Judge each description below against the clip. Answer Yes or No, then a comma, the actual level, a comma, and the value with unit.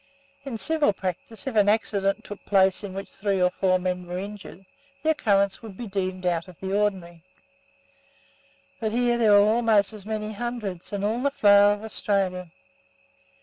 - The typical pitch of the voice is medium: No, high, 200 Hz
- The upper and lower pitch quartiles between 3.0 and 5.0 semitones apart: No, narrow, 2.6 semitones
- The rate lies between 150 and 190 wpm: Yes, average, 175 wpm